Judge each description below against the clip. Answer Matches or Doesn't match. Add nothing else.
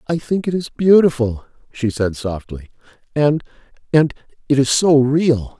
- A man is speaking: Matches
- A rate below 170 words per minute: Matches